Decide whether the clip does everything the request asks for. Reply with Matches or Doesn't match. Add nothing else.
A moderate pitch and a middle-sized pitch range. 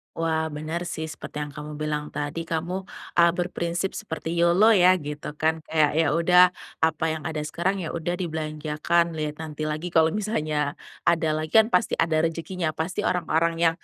Doesn't match